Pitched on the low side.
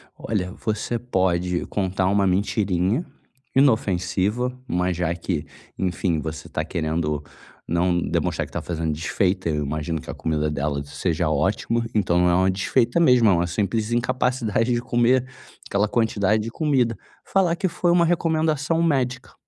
Yes: low, 100 Hz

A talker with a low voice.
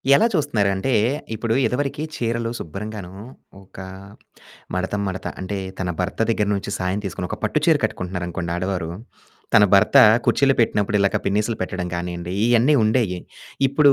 Yes: low, 100 Hz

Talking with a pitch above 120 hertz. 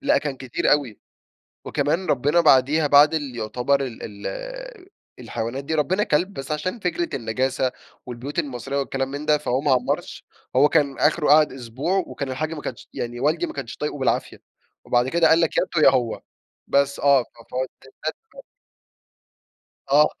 Yes: medium, 140 Hz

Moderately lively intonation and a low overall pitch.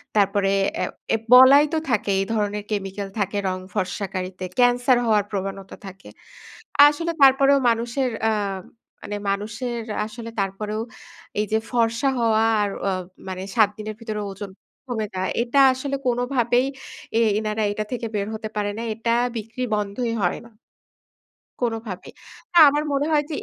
No: average, 3.3 semitones; high, 220 Hz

